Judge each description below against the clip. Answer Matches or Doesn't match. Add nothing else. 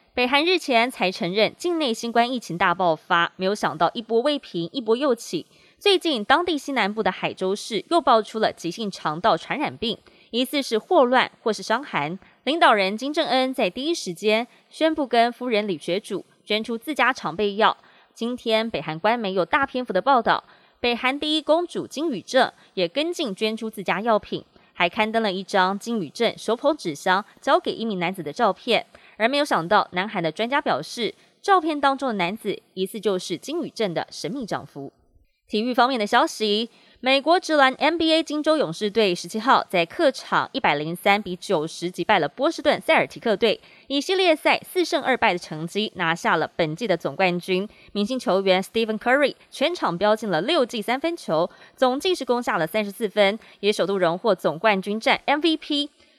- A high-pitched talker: Matches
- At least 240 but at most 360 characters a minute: Matches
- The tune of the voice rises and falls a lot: Matches